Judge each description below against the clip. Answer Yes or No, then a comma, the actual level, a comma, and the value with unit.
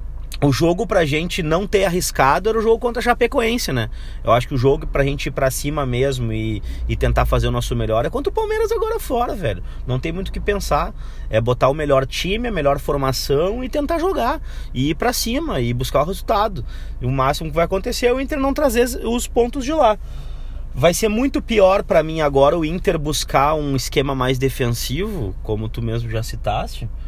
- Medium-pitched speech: Yes, medium, 150 Hz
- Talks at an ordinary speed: No, fast, 220 wpm